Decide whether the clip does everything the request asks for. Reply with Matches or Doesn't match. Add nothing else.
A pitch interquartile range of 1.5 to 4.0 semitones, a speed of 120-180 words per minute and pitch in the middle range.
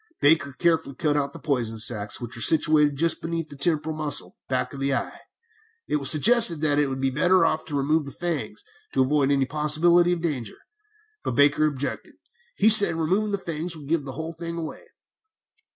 Doesn't match